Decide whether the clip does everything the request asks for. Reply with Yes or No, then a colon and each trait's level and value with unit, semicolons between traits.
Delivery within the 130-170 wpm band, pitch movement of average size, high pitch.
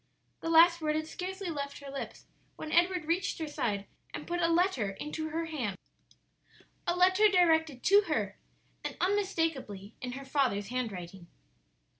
No: average, 155 wpm; wide, 5.7 semitones; very high, 315 Hz